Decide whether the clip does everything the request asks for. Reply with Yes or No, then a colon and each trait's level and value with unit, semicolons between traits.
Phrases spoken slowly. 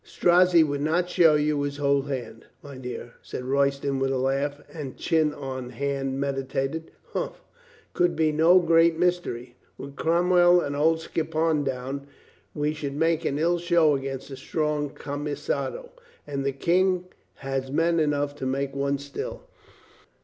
No: average, 155 wpm